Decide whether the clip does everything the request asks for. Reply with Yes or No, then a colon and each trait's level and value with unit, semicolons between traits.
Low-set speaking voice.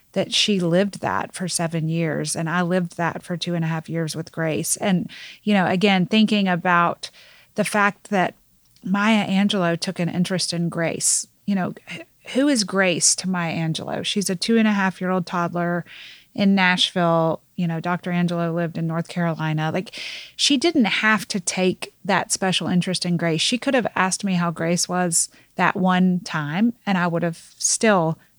No: medium, 180 Hz